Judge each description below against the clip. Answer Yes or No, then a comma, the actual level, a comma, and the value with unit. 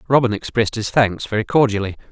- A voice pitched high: No, low, 110 Hz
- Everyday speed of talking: Yes, average, 170 wpm